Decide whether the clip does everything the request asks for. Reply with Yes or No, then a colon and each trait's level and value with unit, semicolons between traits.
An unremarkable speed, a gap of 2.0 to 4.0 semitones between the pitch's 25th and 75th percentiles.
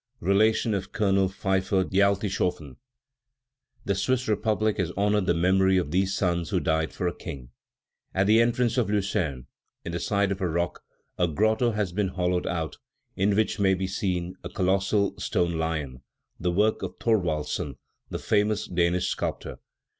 Yes: average, 160 wpm; average, 3.0 semitones